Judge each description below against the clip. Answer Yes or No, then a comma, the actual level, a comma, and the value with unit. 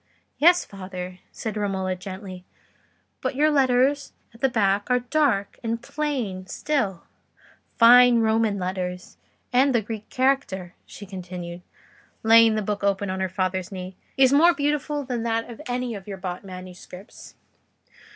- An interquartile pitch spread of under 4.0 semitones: No, average, 5.1 semitones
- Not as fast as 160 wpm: Yes, average, 140 wpm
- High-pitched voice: Yes, high, 215 Hz